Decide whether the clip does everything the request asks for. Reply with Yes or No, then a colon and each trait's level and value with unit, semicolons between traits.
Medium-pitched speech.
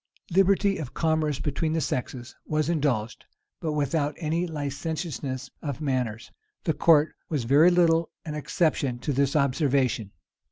Yes: medium, 150 Hz